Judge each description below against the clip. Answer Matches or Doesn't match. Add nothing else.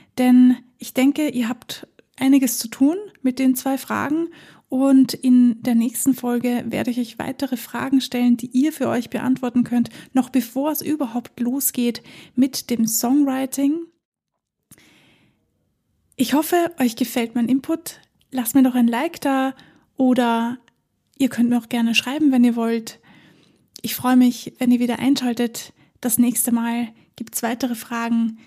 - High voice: Matches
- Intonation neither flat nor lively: Doesn't match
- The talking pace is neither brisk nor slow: Matches